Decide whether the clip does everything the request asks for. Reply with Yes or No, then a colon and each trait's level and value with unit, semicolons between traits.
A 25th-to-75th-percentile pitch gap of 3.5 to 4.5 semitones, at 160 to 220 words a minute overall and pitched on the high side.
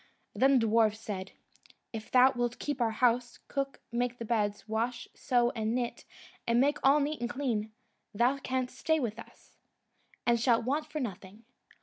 No: average, 2.8 semitones; average, 175 wpm; high, 240 Hz